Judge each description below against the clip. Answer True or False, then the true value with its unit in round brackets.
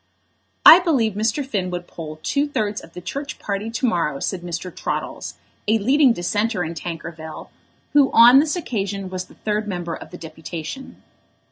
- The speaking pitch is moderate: False (200 Hz)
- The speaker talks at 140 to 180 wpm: True (170 wpm)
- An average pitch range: False (5.9 semitones)